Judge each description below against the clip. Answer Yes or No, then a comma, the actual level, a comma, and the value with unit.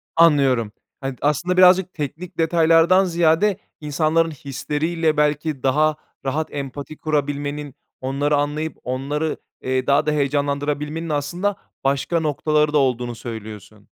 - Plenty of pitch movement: No, average, 2.7 semitones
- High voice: No, medium, 150 Hz